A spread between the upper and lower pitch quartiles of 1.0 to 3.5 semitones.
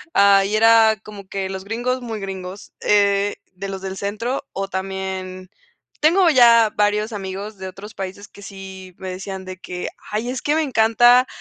Yes: average, 2.8 semitones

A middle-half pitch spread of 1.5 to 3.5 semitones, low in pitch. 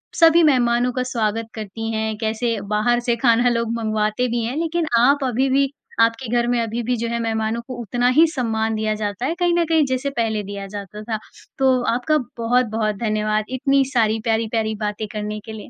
No: narrow, 2.5 semitones; high, 230 Hz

